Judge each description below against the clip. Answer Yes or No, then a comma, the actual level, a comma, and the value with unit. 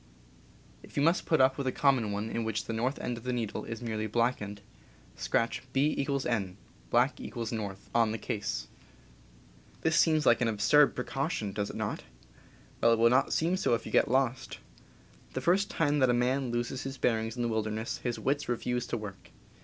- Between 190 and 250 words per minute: Yes, average, 200 wpm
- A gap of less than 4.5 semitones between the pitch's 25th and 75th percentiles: Yes, average, 3.4 semitones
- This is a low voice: Yes, low, 120 Hz